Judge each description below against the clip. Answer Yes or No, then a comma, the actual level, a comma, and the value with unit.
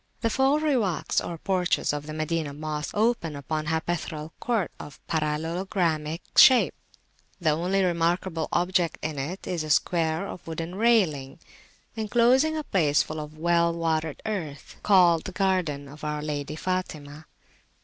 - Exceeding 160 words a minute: No, average, 150 wpm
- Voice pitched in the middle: Yes, medium, 165 Hz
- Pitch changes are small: No, average, 3.7 semitones